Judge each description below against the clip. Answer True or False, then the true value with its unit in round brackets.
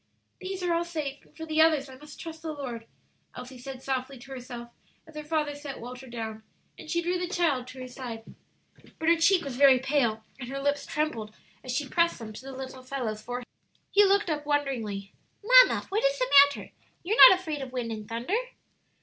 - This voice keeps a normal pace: False (210 wpm)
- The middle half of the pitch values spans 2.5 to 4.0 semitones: False (4.6 semitones)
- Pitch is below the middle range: False (275 Hz)